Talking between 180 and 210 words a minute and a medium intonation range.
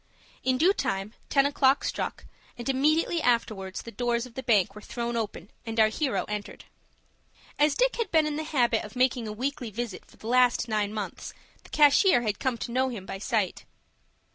Yes: average, 195 wpm; average, 4.1 semitones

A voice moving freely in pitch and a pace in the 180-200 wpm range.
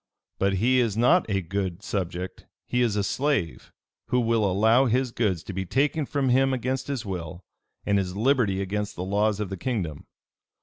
No: average, 4.8 semitones; average, 185 wpm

